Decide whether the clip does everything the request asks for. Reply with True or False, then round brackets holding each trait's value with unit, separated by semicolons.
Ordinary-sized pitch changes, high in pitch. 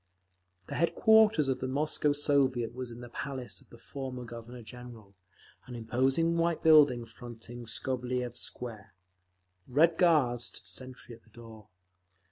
False (3.3 semitones; 125 Hz)